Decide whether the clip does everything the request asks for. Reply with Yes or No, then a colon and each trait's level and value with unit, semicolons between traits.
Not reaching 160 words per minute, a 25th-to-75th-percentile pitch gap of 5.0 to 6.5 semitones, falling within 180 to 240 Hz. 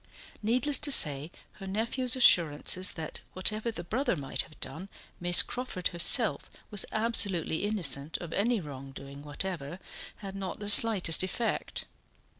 Yes: slow, 135 wpm; wide, 5.5 semitones; medium, 185 Hz